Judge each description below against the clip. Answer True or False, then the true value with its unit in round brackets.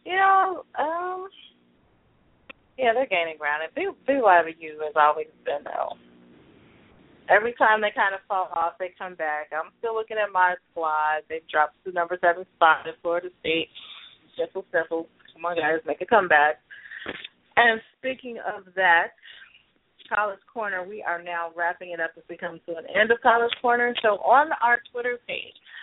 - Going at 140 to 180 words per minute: True (170 wpm)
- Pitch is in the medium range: True (180 Hz)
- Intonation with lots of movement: True (6.2 semitones)